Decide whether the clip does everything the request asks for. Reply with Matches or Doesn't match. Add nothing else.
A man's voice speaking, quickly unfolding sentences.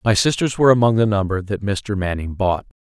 Matches